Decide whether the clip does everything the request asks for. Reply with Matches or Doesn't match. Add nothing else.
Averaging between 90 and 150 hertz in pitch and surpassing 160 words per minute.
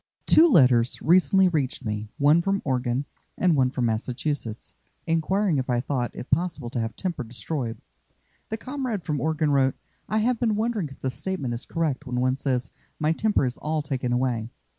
Matches